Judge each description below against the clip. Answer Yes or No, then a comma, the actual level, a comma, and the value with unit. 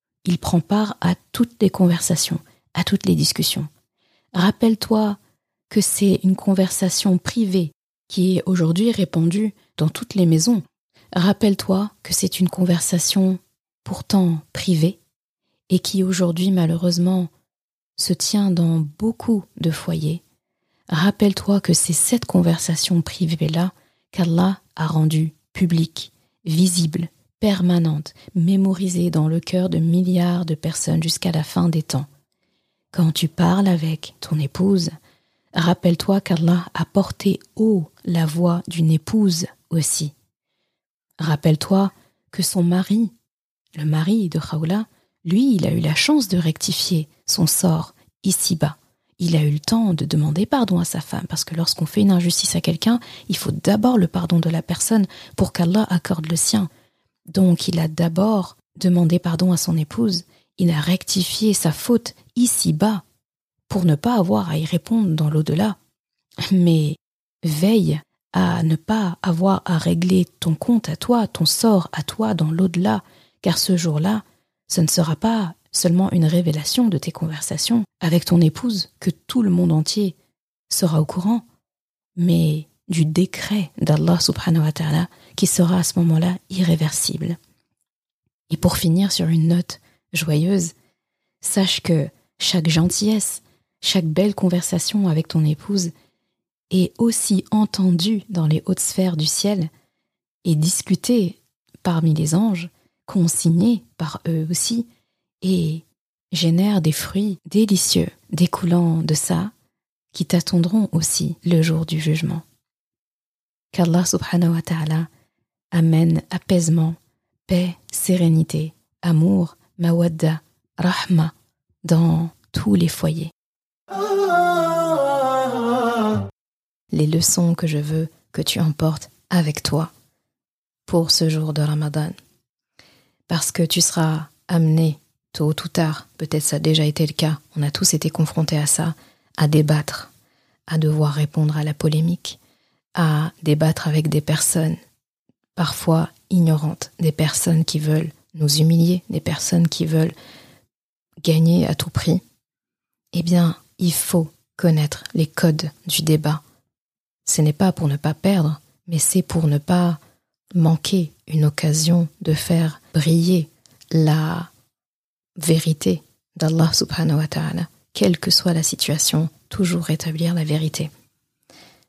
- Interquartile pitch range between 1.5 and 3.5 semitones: Yes, average, 3.0 semitones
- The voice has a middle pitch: Yes, medium, 170 Hz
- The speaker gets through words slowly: Yes, slow, 135 wpm